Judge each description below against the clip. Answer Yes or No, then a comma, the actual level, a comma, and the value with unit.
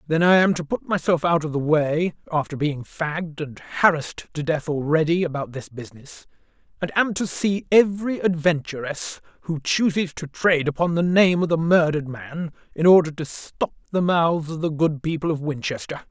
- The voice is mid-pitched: Yes, medium, 160 Hz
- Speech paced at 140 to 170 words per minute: No, average, 180 wpm